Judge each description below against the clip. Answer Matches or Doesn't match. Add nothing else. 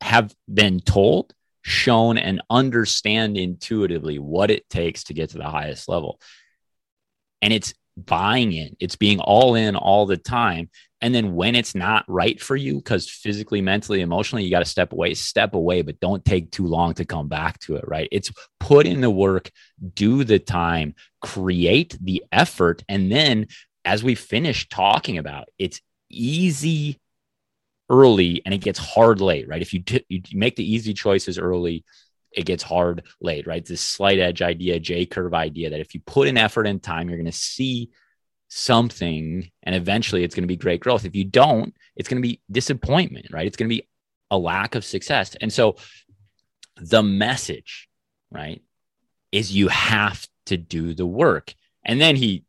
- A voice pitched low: Matches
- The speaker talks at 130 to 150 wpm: Doesn't match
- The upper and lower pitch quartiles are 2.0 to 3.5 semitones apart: Doesn't match